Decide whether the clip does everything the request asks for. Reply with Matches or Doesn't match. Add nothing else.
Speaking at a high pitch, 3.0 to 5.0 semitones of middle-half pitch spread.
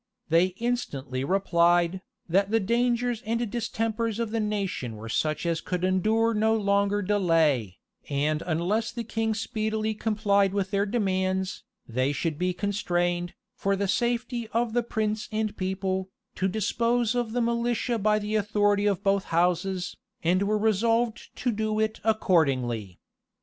Matches